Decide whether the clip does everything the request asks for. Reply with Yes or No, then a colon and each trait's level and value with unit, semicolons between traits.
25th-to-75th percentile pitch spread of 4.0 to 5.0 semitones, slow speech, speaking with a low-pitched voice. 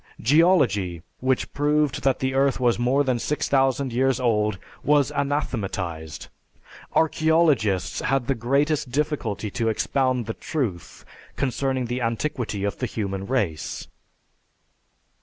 Yes: average, 4.5 semitones; slow, 120 wpm; low, 130 Hz